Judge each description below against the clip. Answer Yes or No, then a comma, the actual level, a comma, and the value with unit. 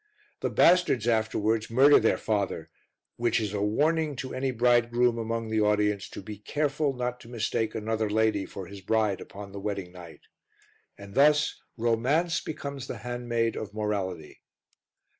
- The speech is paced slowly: No, average, 155 wpm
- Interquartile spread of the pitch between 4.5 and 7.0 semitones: No, average, 3.1 semitones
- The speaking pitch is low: Yes, low, 115 Hz